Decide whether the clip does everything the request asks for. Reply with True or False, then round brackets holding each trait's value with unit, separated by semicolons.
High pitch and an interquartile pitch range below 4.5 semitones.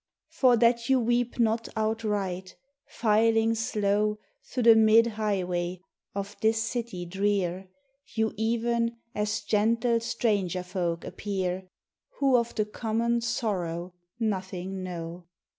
True (215 Hz; 3.6 semitones)